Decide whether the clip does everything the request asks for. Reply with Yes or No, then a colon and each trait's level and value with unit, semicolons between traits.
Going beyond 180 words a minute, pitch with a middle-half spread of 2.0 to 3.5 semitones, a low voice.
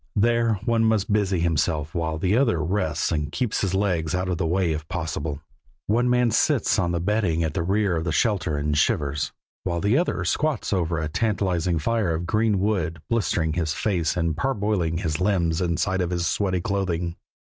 No: average, 190 wpm; average, 4.4 semitones; very low, 90 Hz